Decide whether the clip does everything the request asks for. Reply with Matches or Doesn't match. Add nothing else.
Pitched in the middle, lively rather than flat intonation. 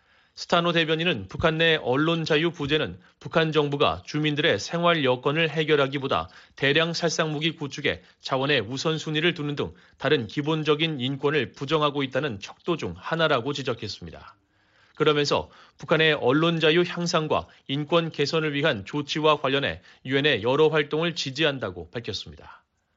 Doesn't match